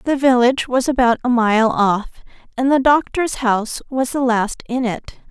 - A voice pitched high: Yes, high, 245 Hz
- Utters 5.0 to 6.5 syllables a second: No, 4.7 syllables/s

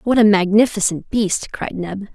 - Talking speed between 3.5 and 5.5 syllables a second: Yes, 4.5 syllables/s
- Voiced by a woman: Yes, female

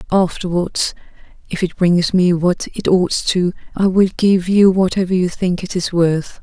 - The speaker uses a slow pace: No, average, 170 wpm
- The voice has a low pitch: No, medium, 180 Hz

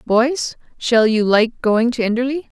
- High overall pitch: Yes, high, 235 Hz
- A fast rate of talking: No, average, 160 wpm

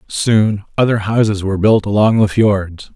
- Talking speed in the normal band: Yes, average, 160 wpm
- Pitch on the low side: Yes, low, 105 Hz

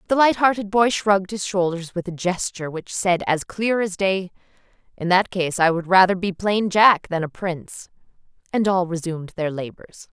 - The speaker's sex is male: No, female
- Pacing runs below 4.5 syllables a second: No, 5.0 syllables/s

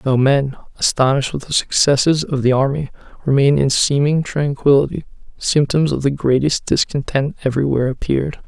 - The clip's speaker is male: Yes, male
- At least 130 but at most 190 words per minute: Yes, average, 150 wpm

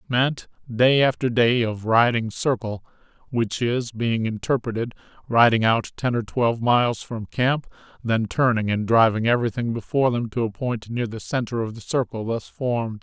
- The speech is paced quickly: No, average, 170 wpm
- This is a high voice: No, low, 115 Hz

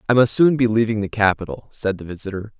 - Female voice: No, male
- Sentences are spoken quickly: Yes, fast, 230 wpm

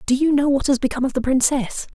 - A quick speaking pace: Yes, fast, 270 wpm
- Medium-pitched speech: No, very high, 270 Hz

